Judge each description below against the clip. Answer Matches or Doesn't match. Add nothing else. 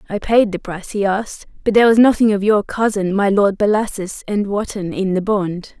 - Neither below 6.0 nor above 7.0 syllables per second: Doesn't match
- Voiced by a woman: Matches